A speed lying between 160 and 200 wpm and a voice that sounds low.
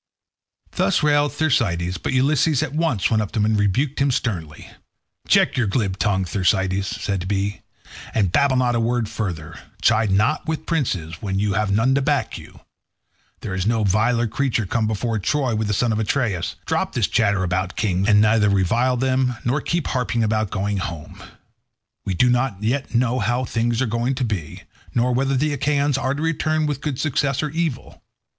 Yes: average, 190 wpm; low, 115 Hz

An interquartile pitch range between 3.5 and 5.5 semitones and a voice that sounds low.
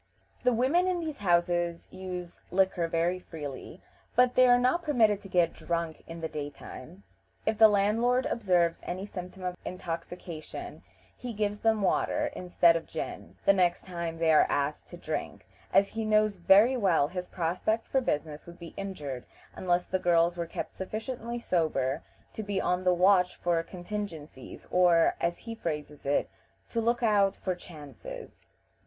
No: average, 4.2 semitones; medium, 180 Hz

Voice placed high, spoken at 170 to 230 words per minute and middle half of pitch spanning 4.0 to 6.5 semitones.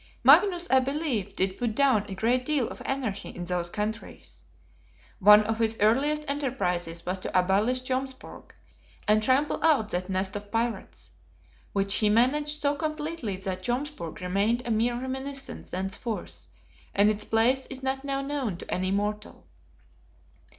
No: high, 230 Hz; average, 150 wpm; average, 5.2 semitones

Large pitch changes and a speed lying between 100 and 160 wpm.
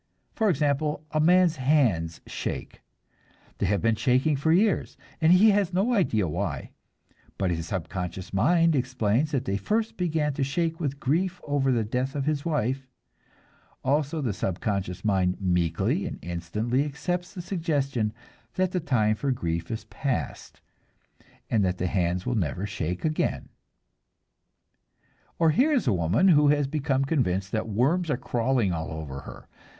Yes: wide, 8.3 semitones; average, 155 wpm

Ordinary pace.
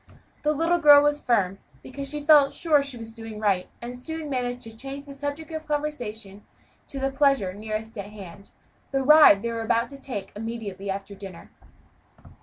Yes: average, 180 wpm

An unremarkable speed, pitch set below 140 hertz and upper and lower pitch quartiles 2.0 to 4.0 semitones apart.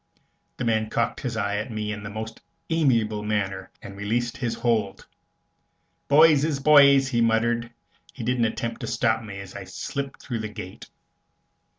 Yes: average, 170 wpm; low, 115 Hz; average, 3.0 semitones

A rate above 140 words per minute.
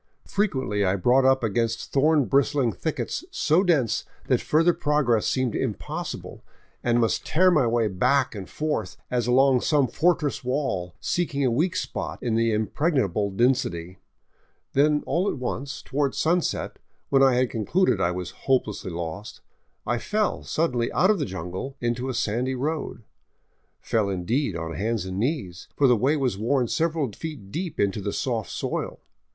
Yes: average, 165 wpm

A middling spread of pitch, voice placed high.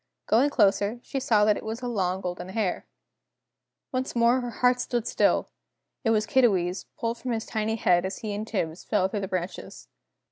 Yes: average, 3.8 semitones; high, 215 Hz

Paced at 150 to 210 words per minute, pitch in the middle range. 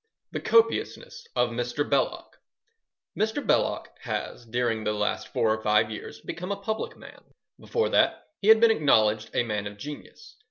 No: average, 165 wpm; low, 120 Hz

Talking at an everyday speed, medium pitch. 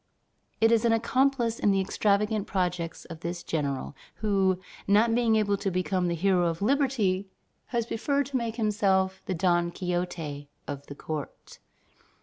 No: average, 155 wpm; high, 195 Hz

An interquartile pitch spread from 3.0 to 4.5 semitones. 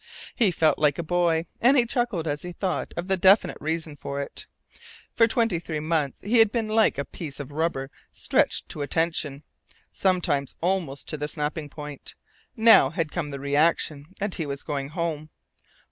Yes: average, 4.2 semitones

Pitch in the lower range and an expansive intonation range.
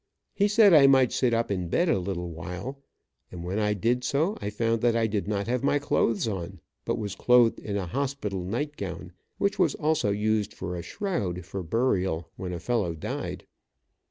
Yes: low, 105 Hz; wide, 6.1 semitones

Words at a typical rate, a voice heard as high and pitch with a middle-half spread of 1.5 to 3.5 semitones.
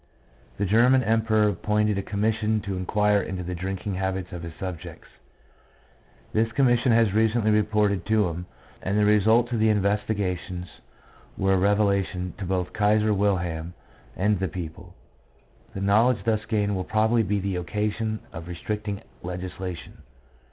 No: average, 150 wpm; low, 100 Hz; average, 2.7 semitones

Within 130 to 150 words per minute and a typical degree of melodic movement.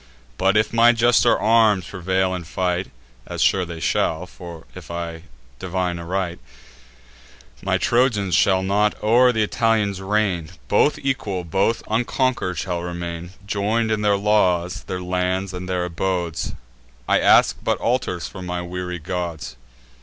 Yes: average, 140 wpm; average, 3.2 semitones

